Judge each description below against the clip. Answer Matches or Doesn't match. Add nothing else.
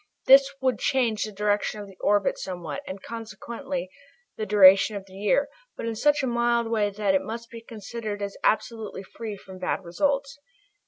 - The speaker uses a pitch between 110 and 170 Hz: Doesn't match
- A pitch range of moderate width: Matches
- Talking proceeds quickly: Doesn't match